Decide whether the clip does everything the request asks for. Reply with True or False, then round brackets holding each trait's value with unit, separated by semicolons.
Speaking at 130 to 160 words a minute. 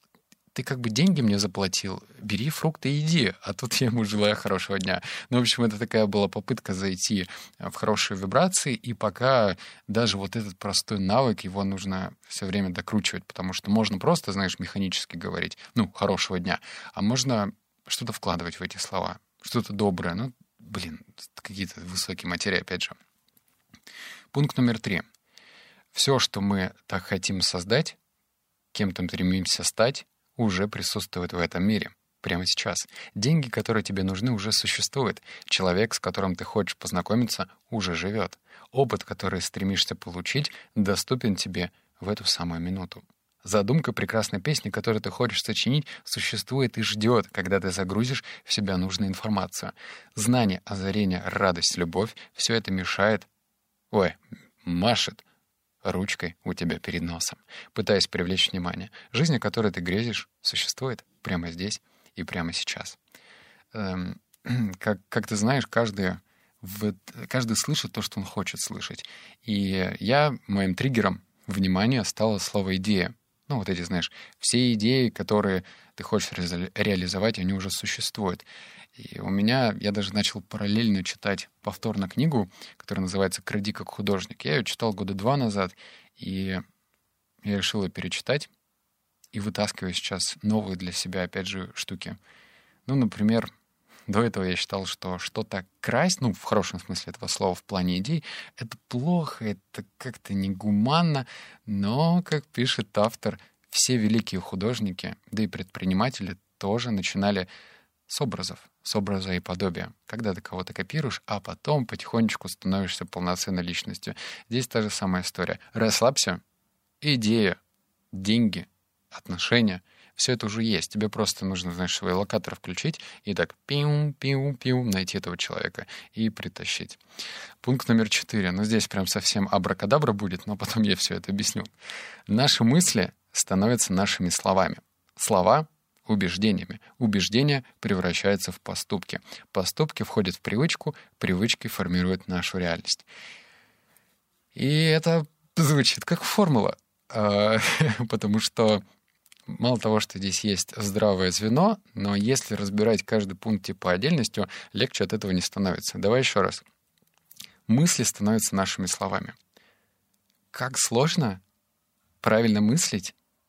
True (140 wpm)